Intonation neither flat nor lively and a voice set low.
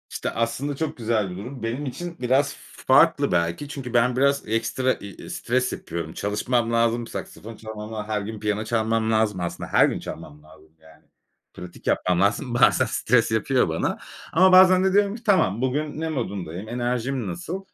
Yes: average, 4.6 semitones; low, 115 Hz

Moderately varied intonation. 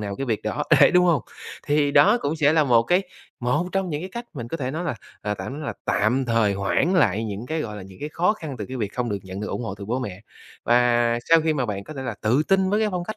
No: wide, 7.0 semitones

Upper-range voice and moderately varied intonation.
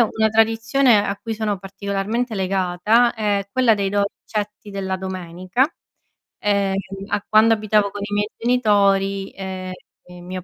No: high, 205 Hz; narrow, 2.2 semitones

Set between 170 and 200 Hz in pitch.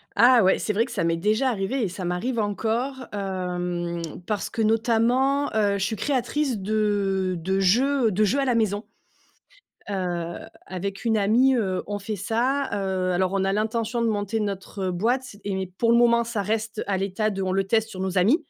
No: high, 210 Hz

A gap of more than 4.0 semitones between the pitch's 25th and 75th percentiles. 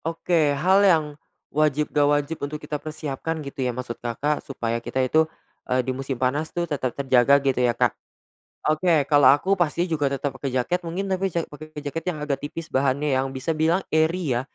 No: average, 3.4 semitones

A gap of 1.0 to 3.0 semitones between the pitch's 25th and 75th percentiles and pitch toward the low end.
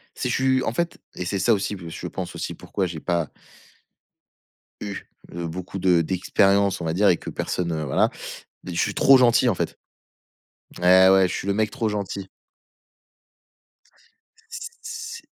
No: average, 3.7 semitones; very low, 95 Hz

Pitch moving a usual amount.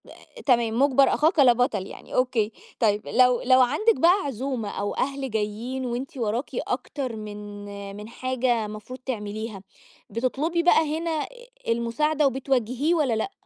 Yes: average, 4.0 semitones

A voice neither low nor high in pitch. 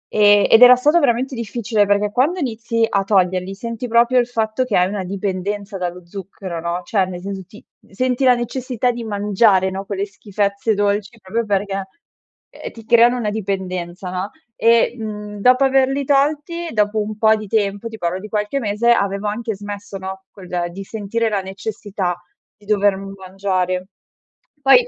No: high, 205 Hz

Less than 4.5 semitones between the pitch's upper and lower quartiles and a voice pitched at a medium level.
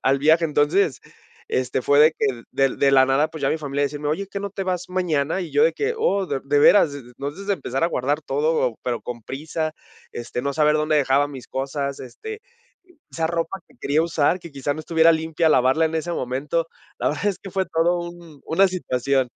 Yes: average, 3.6 semitones; medium, 155 Hz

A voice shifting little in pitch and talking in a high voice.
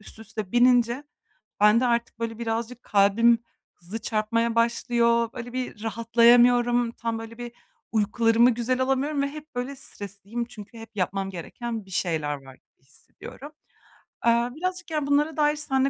Yes: narrow, 2.3 semitones; high, 235 Hz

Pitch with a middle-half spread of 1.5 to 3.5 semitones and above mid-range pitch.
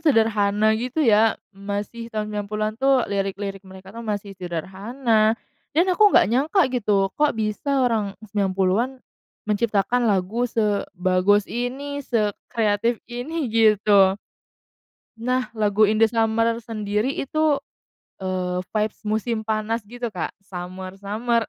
Yes: average, 3.0 semitones; high, 215 Hz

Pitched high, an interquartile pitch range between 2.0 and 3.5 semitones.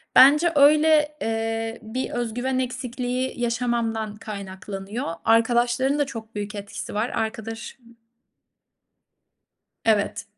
Yes: high, 235 Hz; average, 2.7 semitones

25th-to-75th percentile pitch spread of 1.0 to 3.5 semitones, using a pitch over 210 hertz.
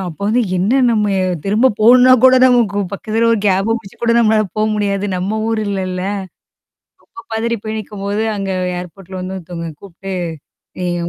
No: average, 2.8 semitones; high, 205 Hz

